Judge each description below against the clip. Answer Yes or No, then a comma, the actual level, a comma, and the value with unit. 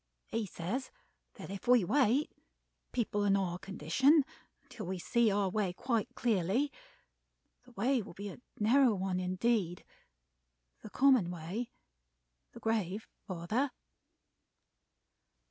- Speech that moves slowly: Yes, slow, 120 wpm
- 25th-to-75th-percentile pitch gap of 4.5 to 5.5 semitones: Yes, average, 4.8 semitones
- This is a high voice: Yes, high, 210 Hz